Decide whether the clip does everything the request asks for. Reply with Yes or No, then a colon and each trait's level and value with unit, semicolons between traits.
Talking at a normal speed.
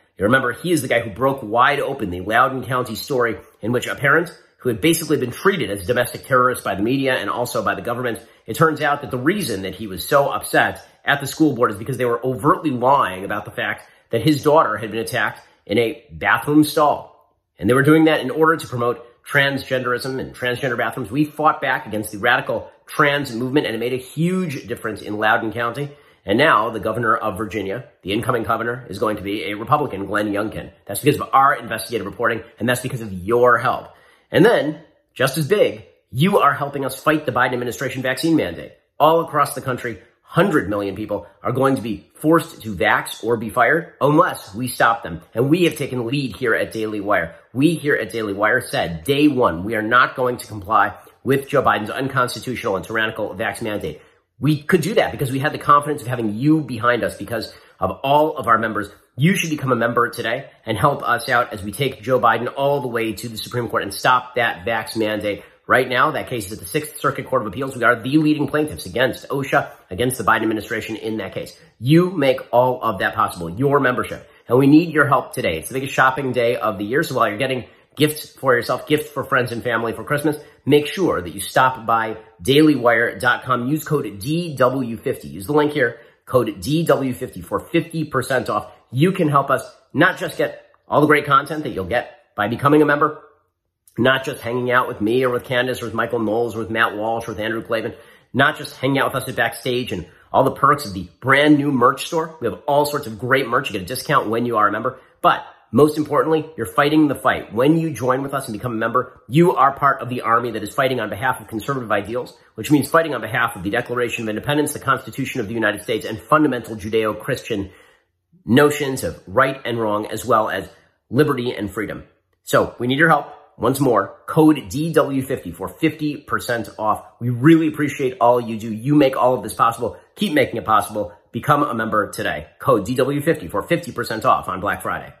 No: fast, 220 wpm